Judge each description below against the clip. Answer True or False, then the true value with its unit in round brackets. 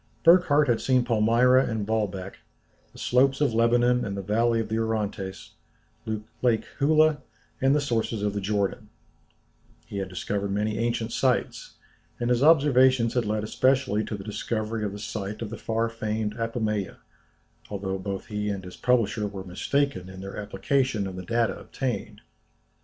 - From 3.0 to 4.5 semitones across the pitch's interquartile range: True (3.3 semitones)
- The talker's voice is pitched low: True (110 Hz)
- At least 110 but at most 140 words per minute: False (165 wpm)